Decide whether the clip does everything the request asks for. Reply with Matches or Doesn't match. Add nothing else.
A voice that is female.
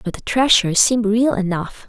Matches